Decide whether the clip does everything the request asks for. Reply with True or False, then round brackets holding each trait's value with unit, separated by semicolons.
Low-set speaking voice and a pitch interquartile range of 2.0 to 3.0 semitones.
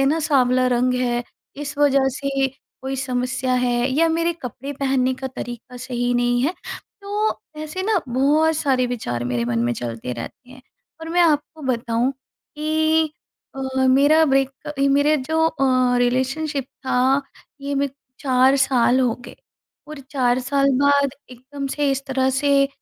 False (265 Hz; 2.6 semitones)